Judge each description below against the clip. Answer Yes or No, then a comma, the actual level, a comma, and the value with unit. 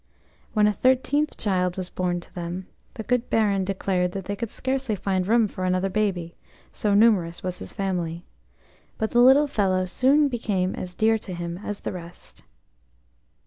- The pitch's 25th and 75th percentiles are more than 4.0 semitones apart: No, average, 3.7 semitones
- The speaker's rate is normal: Yes, average, 175 wpm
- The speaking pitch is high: Yes, high, 195 Hz